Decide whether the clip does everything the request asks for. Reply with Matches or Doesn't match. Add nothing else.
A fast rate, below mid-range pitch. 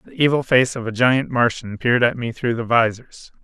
Matches